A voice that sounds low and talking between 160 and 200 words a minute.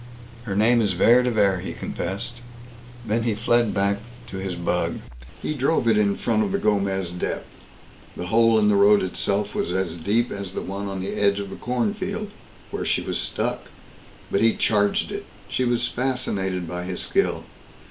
Yes: low, 105 Hz; average, 190 wpm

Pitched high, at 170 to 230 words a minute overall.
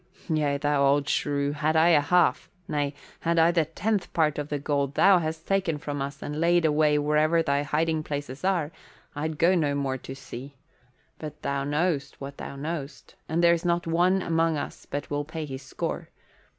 No: medium, 150 Hz; average, 190 wpm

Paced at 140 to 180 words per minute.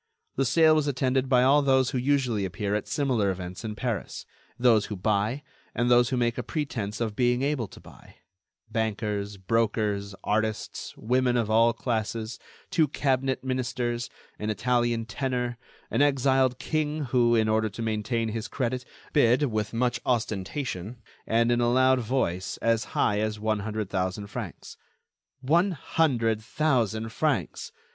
Yes: average, 155 wpm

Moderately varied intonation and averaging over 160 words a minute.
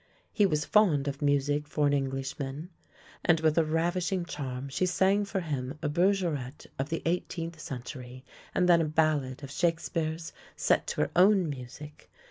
Yes: average, 3.7 semitones; average, 170 wpm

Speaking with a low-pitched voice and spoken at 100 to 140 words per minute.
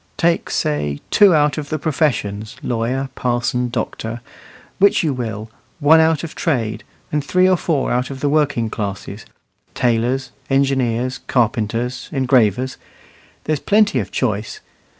Yes: low, 130 Hz; slow, 135 wpm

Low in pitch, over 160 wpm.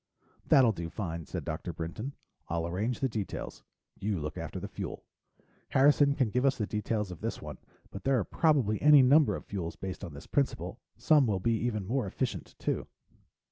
Yes: low, 110 Hz; average, 190 wpm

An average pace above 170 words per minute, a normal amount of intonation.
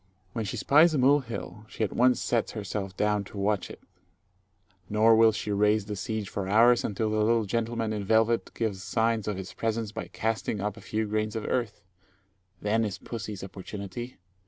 No: average, 190 wpm; narrow, 1.8 semitones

